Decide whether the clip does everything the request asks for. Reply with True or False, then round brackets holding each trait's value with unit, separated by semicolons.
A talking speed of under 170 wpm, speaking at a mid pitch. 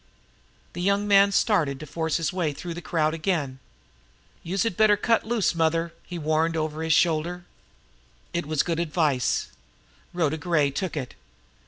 True (160 wpm; 165 Hz)